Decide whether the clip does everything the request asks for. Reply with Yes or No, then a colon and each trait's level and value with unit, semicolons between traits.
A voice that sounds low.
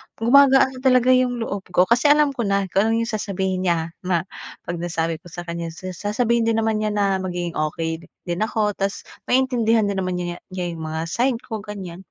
No: high, 200 Hz